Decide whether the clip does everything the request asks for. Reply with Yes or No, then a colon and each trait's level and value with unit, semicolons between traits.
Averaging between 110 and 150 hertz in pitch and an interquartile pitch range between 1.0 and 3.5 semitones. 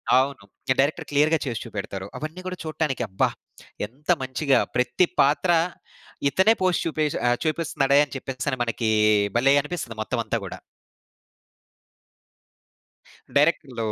No: medium, 140 Hz; average, 4.0 semitones